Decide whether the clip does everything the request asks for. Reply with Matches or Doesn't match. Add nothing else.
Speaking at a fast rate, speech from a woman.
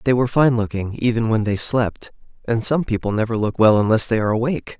Doesn't match